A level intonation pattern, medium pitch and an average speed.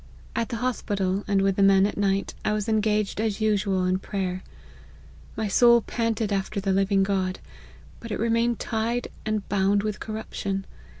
No: narrow, 2.1 semitones; high, 205 Hz; average, 170 wpm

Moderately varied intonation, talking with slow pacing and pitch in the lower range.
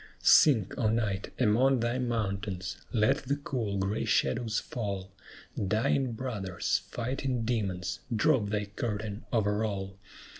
Yes: average, 3.4 semitones; slow, 120 wpm; low, 110 Hz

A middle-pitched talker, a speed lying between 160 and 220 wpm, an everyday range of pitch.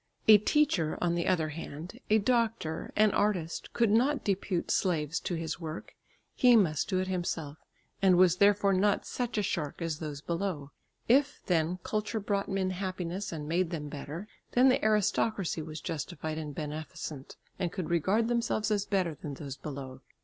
Yes: medium, 180 Hz; average, 170 wpm; average, 4.8 semitones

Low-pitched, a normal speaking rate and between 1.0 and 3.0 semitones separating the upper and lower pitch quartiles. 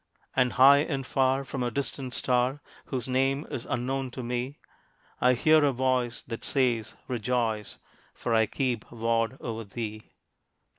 Yes: low, 125 Hz; average, 150 wpm; narrow, 2.4 semitones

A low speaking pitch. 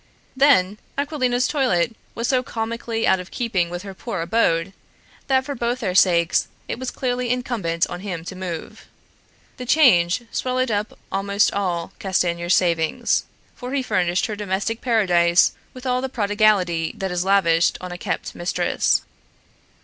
No: high, 200 Hz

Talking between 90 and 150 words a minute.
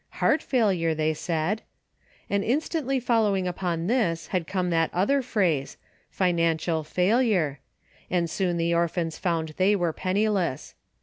Yes: average, 140 wpm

